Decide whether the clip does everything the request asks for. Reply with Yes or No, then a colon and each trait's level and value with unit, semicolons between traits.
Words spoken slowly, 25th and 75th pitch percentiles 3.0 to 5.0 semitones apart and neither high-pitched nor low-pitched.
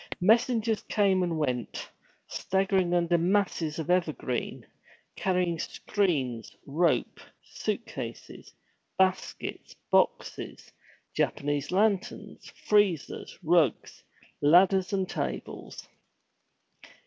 Yes: slow, 80 wpm; average, 3.9 semitones; medium, 180 Hz